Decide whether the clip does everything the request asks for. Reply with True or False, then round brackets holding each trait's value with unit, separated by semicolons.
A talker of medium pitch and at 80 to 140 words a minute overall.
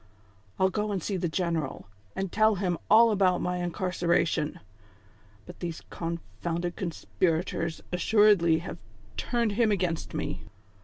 True (180 Hz; 135 wpm)